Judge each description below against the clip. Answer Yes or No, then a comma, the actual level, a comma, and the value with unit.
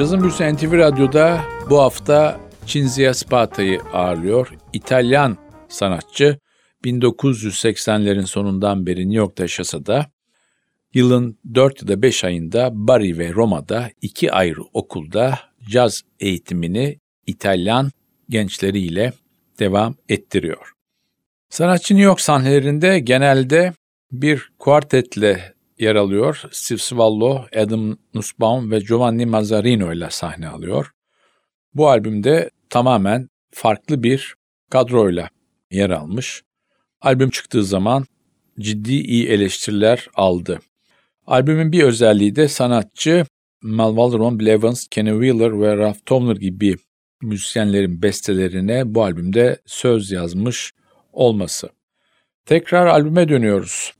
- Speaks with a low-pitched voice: Yes, low, 115 Hz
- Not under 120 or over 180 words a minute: No, average, 105 wpm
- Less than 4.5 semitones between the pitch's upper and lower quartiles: No, average, 4.8 semitones